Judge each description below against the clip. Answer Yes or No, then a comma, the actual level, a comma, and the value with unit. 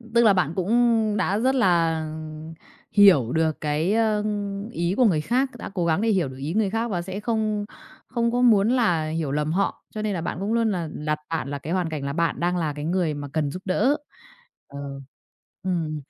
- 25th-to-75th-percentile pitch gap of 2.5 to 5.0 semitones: No, wide, 5.5 semitones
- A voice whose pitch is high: No, medium, 180 Hz